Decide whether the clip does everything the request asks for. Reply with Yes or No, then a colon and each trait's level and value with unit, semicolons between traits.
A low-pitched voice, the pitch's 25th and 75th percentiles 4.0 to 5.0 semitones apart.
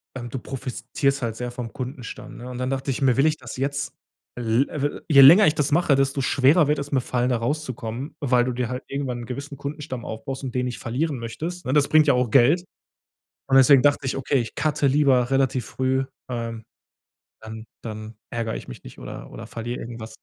No: low, 130 Hz; average, 2.7 semitones